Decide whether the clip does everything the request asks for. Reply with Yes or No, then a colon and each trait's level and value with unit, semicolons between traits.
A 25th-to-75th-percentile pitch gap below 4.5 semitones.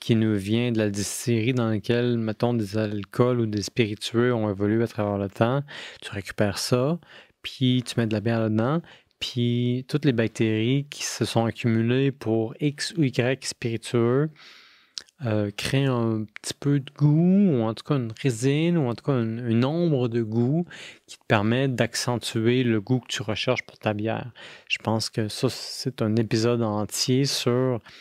Yes: average, 2.8 semitones